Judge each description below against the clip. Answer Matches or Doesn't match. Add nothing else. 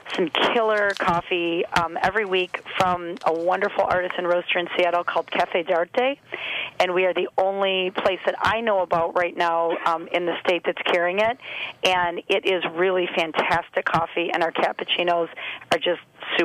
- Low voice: Doesn't match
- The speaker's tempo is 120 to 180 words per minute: Matches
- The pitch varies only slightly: Matches